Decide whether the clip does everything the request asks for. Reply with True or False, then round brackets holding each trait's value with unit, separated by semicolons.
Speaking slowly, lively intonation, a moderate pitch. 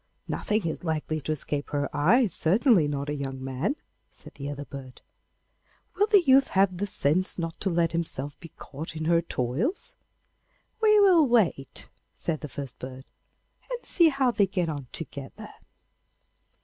False (160 wpm; 7.2 semitones; 165 Hz)